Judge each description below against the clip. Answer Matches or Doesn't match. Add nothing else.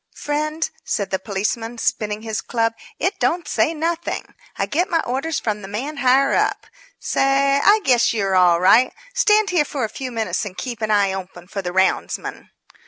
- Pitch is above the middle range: Matches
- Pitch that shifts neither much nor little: Doesn't match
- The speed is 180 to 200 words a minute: Matches